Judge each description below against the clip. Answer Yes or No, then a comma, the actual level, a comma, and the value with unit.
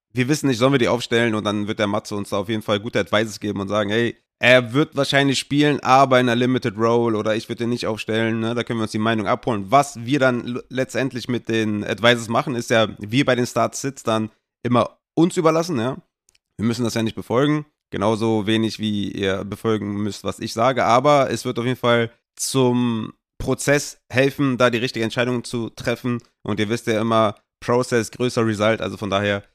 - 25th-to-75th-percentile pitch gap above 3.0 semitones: No, average, 2.7 semitones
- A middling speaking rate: No, fast, 215 wpm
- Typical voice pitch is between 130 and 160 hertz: No, low, 115 Hz